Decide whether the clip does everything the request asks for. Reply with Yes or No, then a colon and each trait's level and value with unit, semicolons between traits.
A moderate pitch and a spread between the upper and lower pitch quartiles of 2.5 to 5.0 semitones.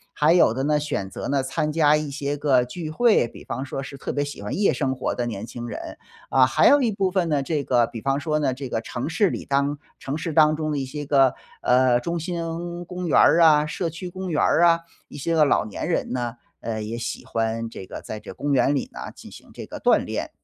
Yes: medium, 145 Hz; average, 4.4 semitones